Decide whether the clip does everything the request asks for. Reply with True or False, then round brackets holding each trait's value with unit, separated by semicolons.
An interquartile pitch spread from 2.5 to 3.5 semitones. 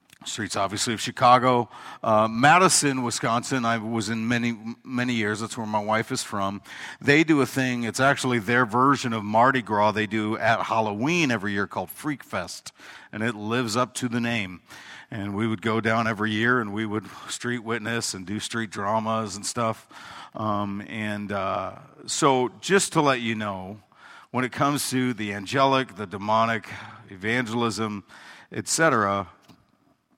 True (2.8 semitones)